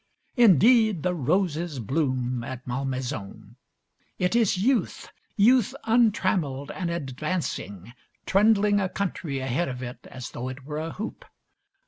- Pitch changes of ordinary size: No, wide, 7.4 semitones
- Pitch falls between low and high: Yes, medium, 160 Hz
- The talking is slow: Yes, slow, 125 wpm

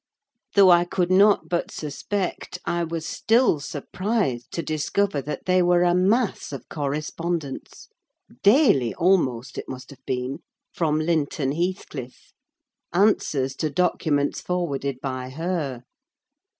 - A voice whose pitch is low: No, medium, 165 Hz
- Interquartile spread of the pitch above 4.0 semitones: Yes, average, 4.7 semitones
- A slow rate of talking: Yes, slow, 115 wpm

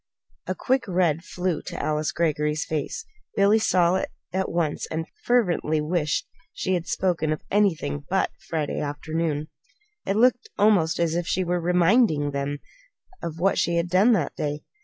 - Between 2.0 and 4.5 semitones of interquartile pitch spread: Yes, average, 3.6 semitones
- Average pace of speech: Yes, average, 165 wpm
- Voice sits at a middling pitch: Yes, medium, 170 Hz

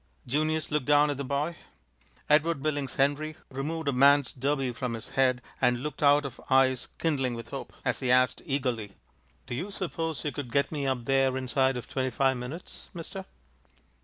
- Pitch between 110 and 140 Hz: Yes, low, 135 Hz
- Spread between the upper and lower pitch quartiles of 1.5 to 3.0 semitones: Yes, average, 2.7 semitones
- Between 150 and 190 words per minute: Yes, average, 185 wpm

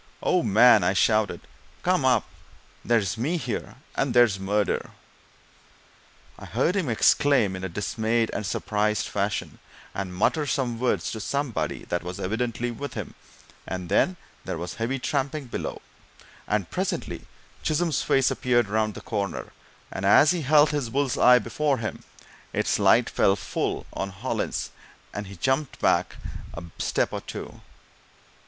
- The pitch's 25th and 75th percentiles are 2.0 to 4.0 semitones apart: No, average, 5.2 semitones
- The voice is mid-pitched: No, low, 115 Hz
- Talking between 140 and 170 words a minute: Yes, average, 150 wpm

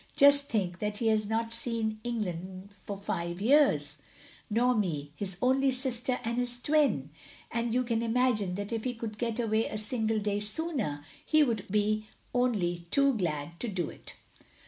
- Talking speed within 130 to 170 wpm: No, average, 180 wpm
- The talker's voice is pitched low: No, high, 220 Hz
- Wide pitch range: No, average, 4.1 semitones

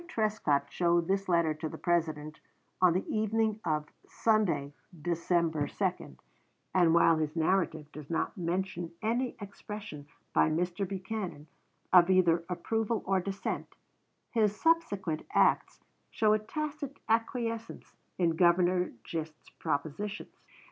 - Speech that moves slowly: Yes, slow, 120 wpm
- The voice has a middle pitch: Yes, medium, 180 Hz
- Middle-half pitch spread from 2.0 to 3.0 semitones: No, average, 4.6 semitones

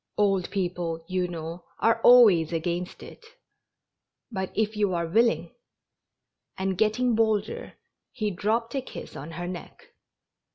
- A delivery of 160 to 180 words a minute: No, average, 150 wpm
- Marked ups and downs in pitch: No, average, 4.1 semitones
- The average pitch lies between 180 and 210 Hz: Yes, high, 190 Hz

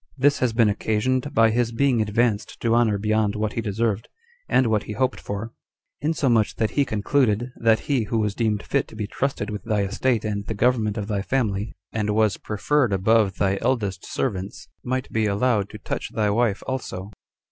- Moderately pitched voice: No, low, 110 Hz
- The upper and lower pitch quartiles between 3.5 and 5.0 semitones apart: No, average, 2.9 semitones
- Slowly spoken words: No, average, 190 wpm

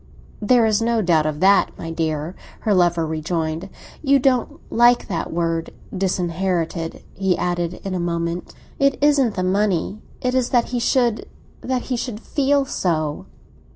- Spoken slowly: No, average, 155 wpm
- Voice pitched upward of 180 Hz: Yes, high, 190 Hz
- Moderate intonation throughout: No, wide, 6.1 semitones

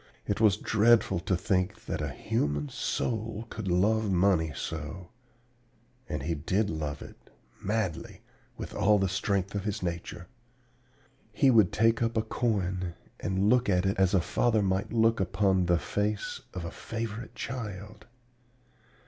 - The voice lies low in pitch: Yes, low, 100 Hz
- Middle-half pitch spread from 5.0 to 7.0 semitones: No, average, 3.4 semitones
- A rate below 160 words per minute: Yes, average, 150 wpm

